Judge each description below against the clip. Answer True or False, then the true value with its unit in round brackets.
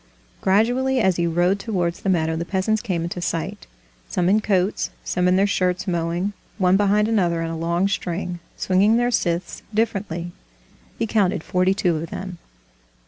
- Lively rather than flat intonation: False (3.0 semitones)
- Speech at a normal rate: True (170 wpm)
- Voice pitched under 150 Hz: False (185 Hz)